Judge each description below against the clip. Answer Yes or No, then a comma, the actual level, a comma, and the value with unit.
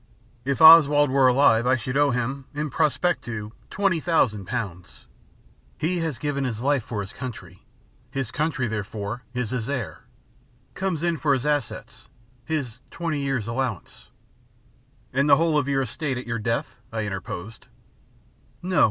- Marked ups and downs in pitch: No, average, 4.4 semitones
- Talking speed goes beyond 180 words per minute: No, average, 155 wpm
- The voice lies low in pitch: Yes, low, 130 Hz